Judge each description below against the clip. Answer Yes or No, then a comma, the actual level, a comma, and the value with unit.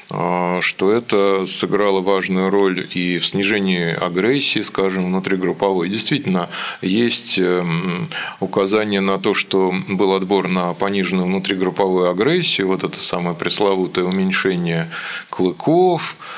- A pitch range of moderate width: No, narrow, 1.6 semitones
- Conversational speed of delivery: No, slow, 105 wpm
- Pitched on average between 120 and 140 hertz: No, very low, 95 Hz